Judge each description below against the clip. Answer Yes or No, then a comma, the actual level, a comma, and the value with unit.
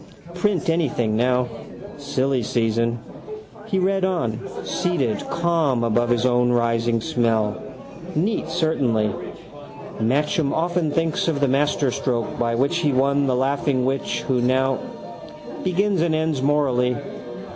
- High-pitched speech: No, low, 135 Hz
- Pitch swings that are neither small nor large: Yes, average, 5.0 semitones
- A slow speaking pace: Yes, slow, 125 wpm